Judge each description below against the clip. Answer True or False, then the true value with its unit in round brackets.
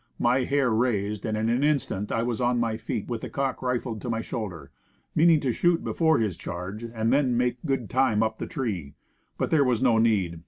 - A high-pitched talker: False (120 Hz)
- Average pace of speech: False (220 wpm)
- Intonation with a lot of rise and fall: False (3.3 semitones)